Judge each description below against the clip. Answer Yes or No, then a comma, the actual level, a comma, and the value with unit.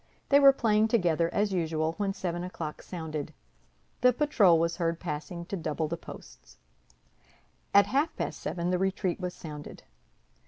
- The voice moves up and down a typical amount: Yes, average, 3.9 semitones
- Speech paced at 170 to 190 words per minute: No, average, 155 wpm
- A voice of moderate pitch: Yes, medium, 175 Hz